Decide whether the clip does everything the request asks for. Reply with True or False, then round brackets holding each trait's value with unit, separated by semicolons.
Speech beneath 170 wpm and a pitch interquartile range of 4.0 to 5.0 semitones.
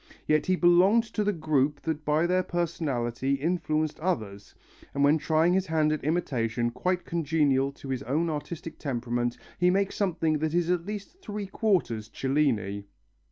True (160 wpm; 4.7 semitones)